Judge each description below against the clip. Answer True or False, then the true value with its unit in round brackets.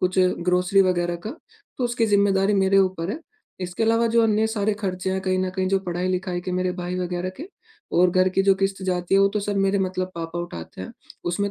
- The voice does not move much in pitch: True (1.9 semitones)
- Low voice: False (190 Hz)